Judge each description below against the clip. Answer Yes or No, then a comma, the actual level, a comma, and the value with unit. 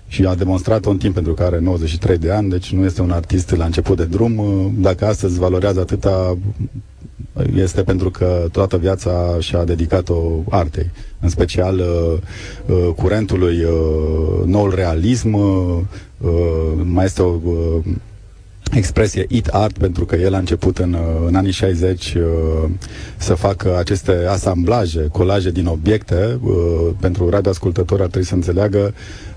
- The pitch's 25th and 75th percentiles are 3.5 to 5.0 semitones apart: No, narrow, 2.4 semitones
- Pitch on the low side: Yes, very low, 95 Hz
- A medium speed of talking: Yes, average, 145 wpm